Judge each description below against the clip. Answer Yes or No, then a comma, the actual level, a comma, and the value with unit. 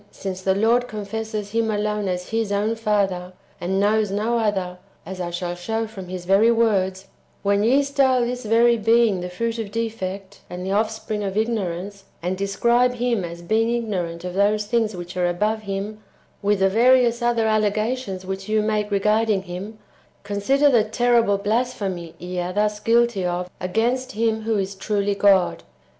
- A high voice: Yes, high, 210 Hz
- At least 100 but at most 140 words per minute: No, average, 180 wpm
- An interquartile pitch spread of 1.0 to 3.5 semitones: Yes, average, 3.0 semitones